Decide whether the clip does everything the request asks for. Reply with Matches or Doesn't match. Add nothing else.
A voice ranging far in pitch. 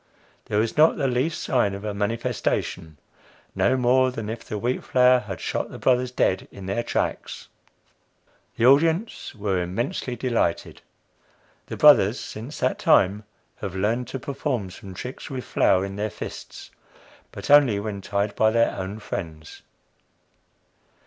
Doesn't match